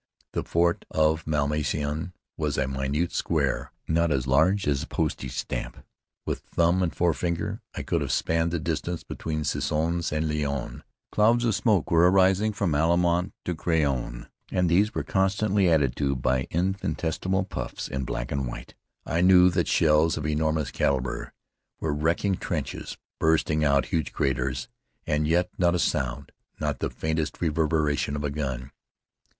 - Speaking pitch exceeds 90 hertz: No, very low, 80 Hz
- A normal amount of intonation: Yes, average, 3.3 semitones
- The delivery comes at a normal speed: Yes, average, 155 wpm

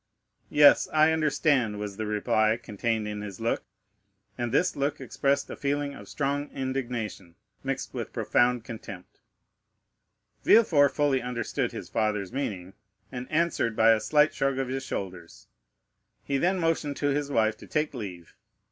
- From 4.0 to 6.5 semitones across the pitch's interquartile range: Yes, average, 5.0 semitones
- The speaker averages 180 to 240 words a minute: No, average, 150 wpm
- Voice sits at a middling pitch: No, low, 125 Hz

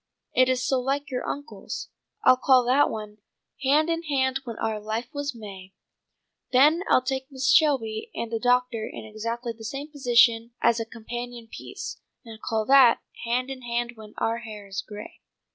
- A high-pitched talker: Yes, high, 240 Hz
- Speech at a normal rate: Yes, average, 180 wpm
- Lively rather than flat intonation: No, average, 3.0 semitones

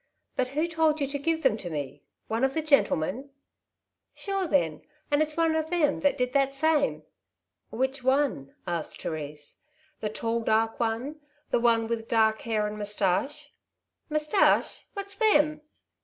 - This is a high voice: Yes, very high, 265 Hz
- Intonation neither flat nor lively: No, wide, 5.9 semitones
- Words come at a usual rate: Yes, average, 185 wpm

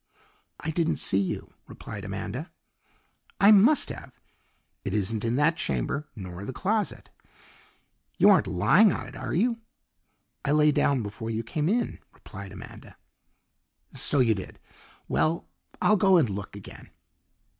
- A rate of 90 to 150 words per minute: Yes, average, 145 wpm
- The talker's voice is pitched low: No, medium, 145 Hz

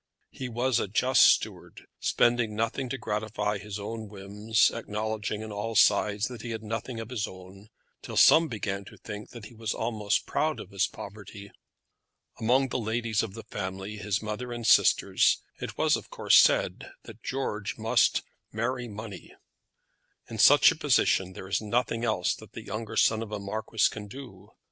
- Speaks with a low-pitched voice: Yes, low, 110 Hz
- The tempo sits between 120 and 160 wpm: No, average, 175 wpm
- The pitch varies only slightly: Yes, narrow, 2.1 semitones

